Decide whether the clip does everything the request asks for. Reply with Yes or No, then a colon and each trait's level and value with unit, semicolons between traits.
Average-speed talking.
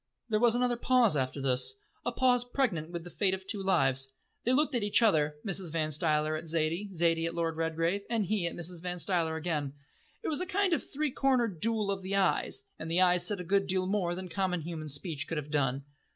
No: fast, 225 wpm